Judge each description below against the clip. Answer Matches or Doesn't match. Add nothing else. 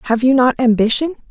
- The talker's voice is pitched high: Matches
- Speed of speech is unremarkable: Matches